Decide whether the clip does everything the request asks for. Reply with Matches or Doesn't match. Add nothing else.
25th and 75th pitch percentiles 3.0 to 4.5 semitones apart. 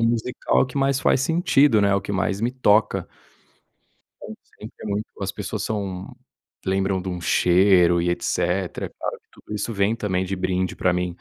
Matches